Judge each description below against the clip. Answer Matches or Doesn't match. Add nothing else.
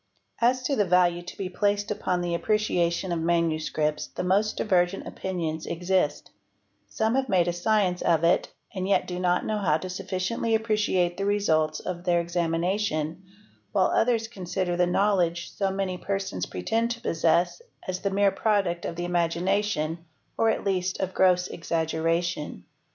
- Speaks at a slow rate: Doesn't match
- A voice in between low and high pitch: Matches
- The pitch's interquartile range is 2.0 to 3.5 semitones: Matches